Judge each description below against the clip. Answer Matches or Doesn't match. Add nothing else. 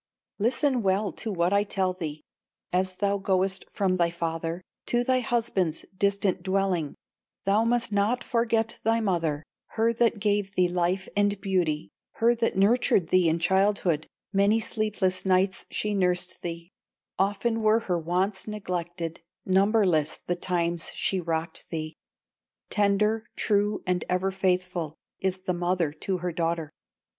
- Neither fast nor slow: Matches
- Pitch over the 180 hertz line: Matches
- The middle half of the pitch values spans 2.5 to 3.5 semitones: Matches